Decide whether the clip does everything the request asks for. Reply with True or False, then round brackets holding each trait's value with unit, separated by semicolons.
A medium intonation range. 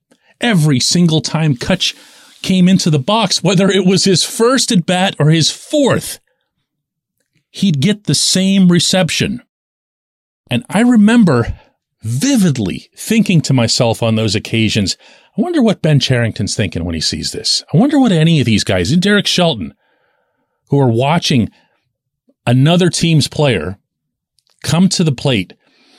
False (7.6 semitones)